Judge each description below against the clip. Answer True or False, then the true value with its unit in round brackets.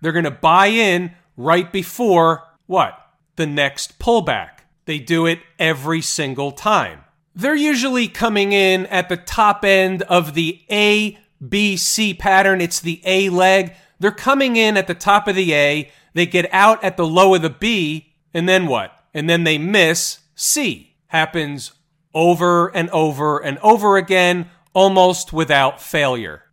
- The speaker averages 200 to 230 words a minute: False (160 wpm)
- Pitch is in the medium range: True (175 Hz)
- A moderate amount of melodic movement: True (3.5 semitones)